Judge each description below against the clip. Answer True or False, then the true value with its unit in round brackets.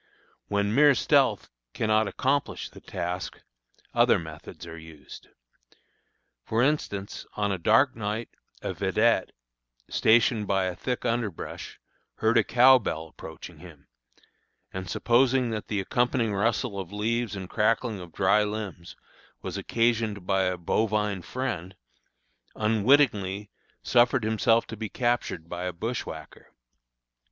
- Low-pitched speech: True (105 Hz)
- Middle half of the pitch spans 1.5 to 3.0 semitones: False (4.0 semitones)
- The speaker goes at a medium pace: False (125 wpm)